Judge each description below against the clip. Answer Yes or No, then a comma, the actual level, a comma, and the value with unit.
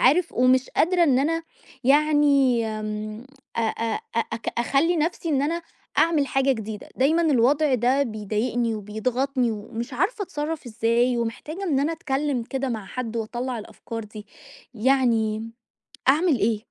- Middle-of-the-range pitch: No, very high, 255 Hz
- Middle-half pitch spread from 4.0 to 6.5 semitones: Yes, average, 4.5 semitones